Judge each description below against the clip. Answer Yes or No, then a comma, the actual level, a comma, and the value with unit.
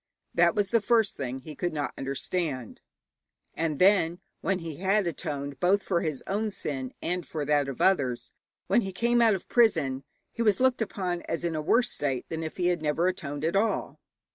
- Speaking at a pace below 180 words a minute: No, average, 200 wpm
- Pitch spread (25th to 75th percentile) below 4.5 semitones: No, average, 5.2 semitones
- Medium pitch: Yes, medium, 170 Hz